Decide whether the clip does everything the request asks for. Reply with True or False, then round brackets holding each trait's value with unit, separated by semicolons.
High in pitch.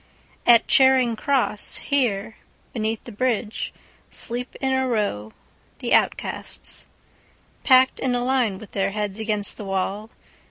True (225 Hz)